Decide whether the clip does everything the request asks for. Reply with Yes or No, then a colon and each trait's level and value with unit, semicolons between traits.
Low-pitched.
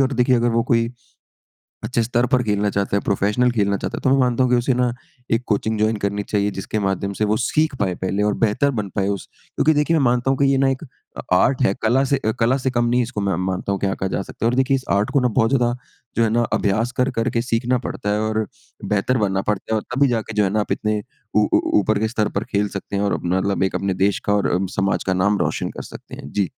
Yes: low, 110 Hz